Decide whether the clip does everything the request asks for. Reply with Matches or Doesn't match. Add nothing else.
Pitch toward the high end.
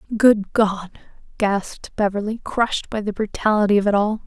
Matches